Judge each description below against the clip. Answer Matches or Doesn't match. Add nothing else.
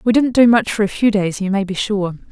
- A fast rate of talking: Matches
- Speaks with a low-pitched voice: Doesn't match